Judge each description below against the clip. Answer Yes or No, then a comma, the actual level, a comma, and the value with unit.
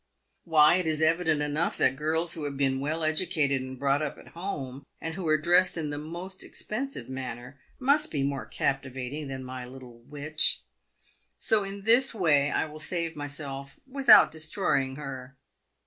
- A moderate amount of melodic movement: Yes, average, 3.8 semitones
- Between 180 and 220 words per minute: No, average, 170 wpm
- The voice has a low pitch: No, medium, 150 Hz